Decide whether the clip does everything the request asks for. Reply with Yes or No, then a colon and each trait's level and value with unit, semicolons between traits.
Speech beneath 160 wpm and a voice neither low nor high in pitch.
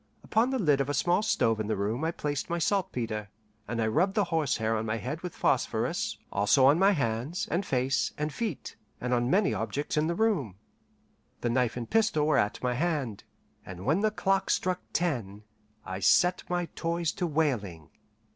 No: average, 195 wpm; medium, 145 Hz